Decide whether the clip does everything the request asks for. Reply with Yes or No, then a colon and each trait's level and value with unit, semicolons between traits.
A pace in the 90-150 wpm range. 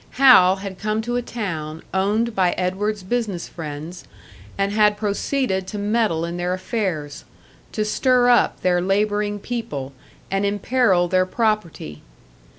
Yes: average, 140 wpm